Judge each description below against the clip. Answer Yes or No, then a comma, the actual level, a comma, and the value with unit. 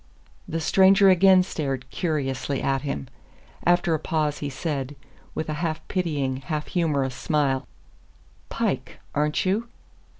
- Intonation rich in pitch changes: No, average, 4.2 semitones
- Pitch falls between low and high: Yes, medium, 150 Hz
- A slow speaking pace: Yes, slow, 130 wpm